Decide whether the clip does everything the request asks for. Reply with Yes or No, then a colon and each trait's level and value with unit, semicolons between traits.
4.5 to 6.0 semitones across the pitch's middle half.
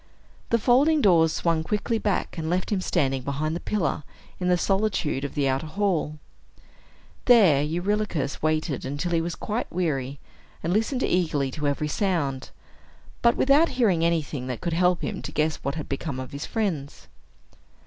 Yes: wide, 5.5 semitones